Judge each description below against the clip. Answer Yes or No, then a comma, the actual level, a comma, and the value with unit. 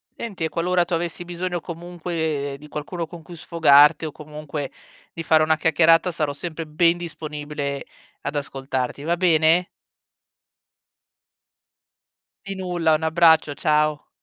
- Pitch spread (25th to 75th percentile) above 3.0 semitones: No, narrow, 2.4 semitones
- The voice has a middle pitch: Yes, medium, 160 Hz